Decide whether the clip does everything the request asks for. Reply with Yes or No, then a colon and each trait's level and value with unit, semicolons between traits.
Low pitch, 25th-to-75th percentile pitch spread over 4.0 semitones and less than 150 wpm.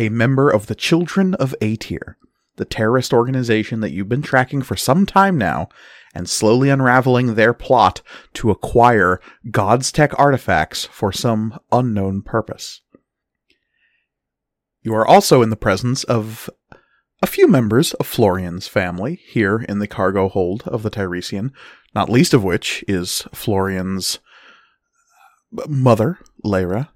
Yes: low, 115 Hz; average, 4.6 semitones; slow, 135 wpm